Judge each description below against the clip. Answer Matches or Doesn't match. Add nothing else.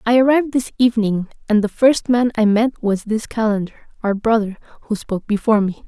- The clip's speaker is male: Doesn't match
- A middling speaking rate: Matches